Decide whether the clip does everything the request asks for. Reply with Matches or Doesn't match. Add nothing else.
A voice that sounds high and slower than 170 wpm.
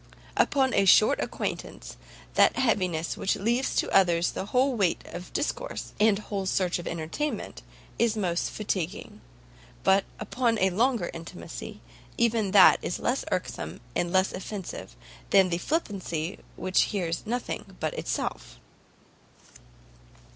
Matches